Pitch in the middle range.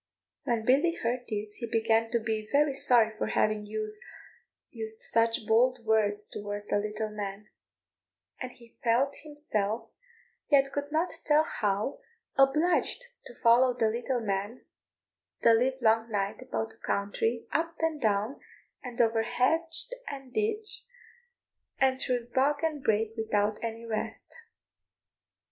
No: high, 230 Hz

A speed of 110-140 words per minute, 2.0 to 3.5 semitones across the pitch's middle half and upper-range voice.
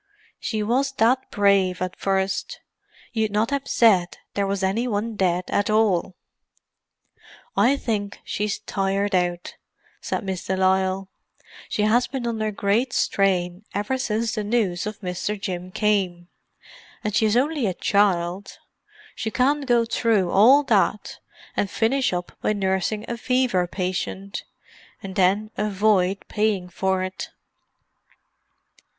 Yes: slow, 135 wpm; average, 3.0 semitones; high, 205 Hz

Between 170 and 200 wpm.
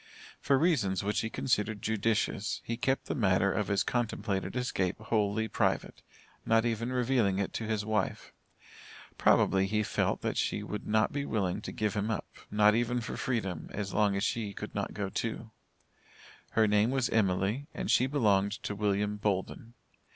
Yes: average, 175 wpm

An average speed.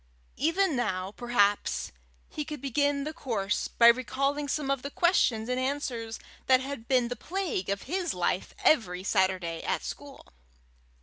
Yes: average, 150 wpm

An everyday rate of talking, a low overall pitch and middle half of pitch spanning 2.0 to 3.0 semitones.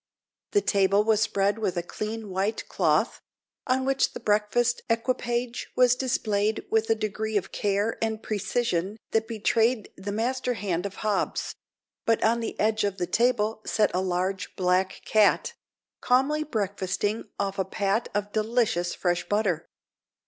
No: average, 150 wpm; high, 215 Hz; narrow, 2.6 semitones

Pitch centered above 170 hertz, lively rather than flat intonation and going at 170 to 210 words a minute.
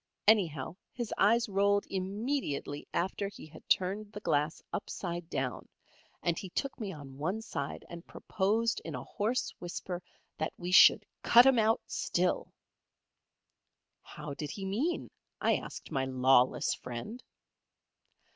No: high, 190 Hz; wide, 6.0 semitones; slow, 135 wpm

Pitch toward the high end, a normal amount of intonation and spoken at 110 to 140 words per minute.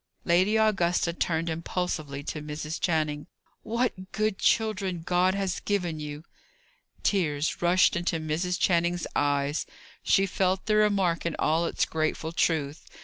No: medium, 170 Hz; average, 3.2 semitones; slow, 135 wpm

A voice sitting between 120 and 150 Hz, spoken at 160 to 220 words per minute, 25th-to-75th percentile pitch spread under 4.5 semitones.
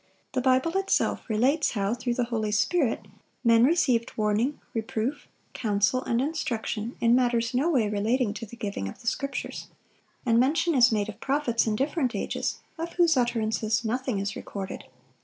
No: high, 235 Hz; average, 170 wpm; average, 3.4 semitones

